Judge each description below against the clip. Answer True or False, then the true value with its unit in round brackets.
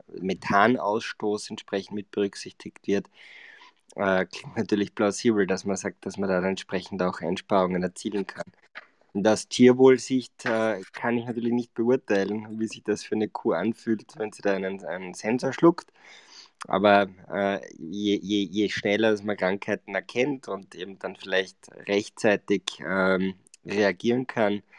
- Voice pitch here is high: False (105 Hz)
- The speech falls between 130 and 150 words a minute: True (145 wpm)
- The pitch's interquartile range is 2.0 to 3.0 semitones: True (2.6 semitones)